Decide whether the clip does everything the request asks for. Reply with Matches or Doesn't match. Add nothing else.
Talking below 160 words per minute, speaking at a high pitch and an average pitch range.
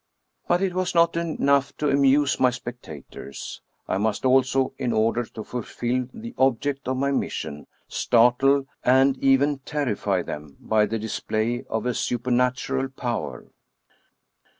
Doesn't match